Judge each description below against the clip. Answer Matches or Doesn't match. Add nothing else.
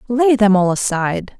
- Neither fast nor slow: Matches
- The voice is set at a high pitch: Matches